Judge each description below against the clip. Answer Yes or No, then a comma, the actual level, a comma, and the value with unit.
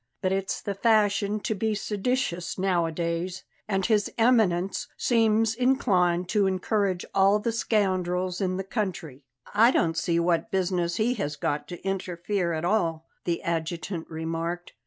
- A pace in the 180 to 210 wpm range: No, average, 145 wpm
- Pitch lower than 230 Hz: Yes, medium, 185 Hz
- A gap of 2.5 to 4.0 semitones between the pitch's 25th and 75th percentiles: Yes, average, 3.6 semitones